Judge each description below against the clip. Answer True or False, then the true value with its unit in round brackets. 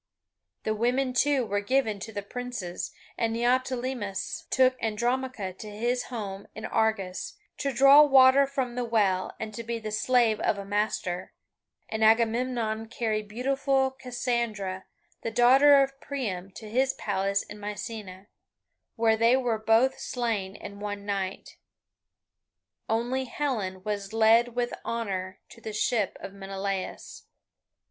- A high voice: True (225 Hz)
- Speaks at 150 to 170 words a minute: False (140 wpm)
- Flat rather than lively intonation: False (3.6 semitones)